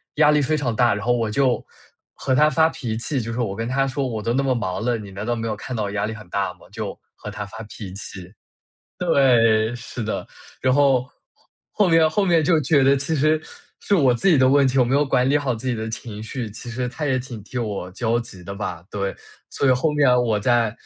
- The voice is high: No, low, 120 Hz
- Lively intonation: No, average, 4.0 semitones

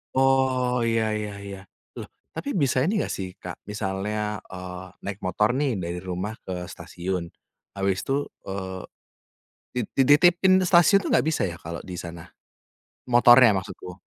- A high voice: No, low, 105 Hz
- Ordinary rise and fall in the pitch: No, wide, 6.2 semitones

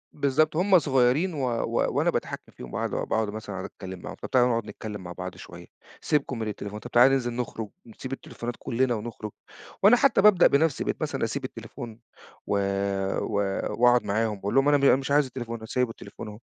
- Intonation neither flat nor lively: Yes, average, 4.3 semitones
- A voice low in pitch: Yes, low, 120 Hz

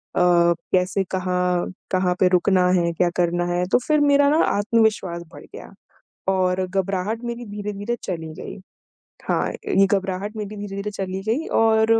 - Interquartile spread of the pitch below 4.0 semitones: Yes, average, 2.8 semitones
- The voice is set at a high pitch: Yes, high, 195 Hz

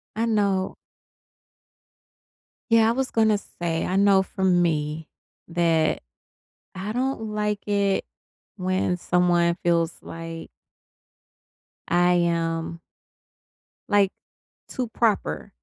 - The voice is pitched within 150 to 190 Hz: Yes, medium, 185 Hz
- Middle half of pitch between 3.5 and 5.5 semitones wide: Yes, average, 3.8 semitones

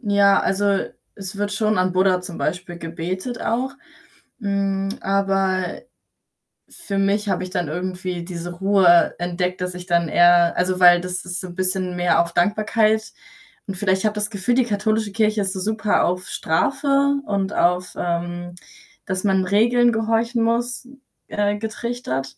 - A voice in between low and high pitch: No, high, 195 Hz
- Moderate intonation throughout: Yes, average, 3.0 semitones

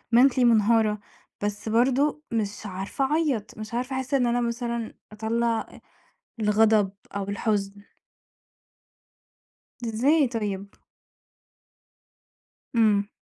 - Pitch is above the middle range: Yes, high, 225 Hz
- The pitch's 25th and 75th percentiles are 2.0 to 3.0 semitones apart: Yes, average, 2.7 semitones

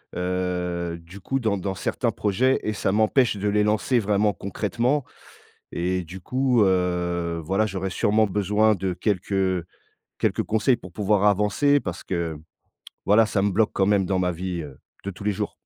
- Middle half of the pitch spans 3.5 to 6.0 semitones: No, average, 2.8 semitones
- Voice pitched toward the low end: Yes, low, 100 Hz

